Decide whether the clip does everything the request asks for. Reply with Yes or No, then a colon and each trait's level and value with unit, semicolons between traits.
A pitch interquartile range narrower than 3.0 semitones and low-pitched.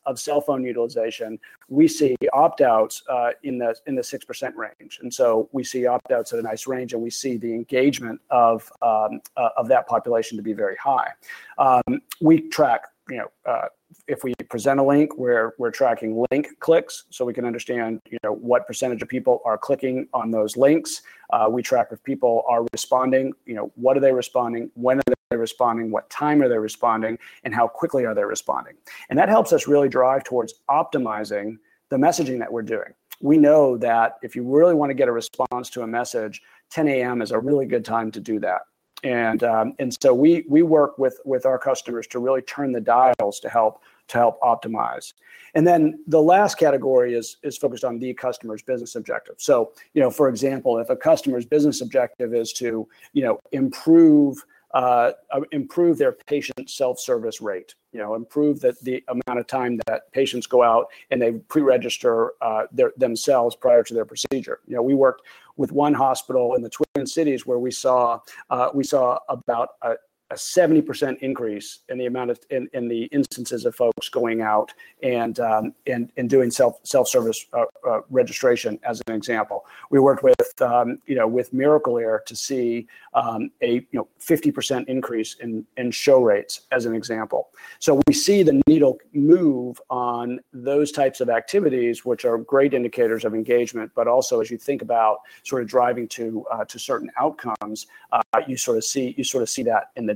No: average, 4.1 semitones; low, 130 Hz